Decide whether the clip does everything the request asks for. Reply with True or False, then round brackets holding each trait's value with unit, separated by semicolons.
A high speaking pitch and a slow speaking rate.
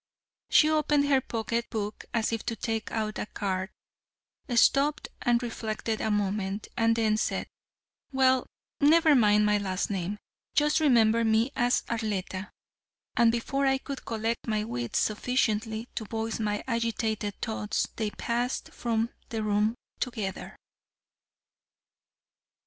True (225 Hz; 130 wpm)